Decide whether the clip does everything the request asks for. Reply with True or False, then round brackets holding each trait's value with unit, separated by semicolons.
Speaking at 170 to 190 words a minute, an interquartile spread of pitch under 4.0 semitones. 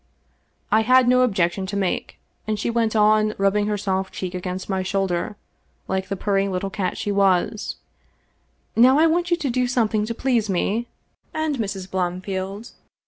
True (180 wpm; 3.5 semitones)